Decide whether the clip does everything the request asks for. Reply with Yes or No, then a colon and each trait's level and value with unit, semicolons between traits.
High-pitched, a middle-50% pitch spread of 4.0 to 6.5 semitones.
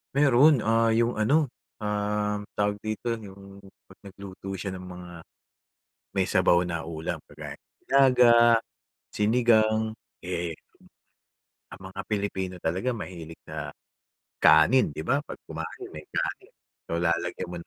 No: low, 105 Hz; average, 4.3 semitones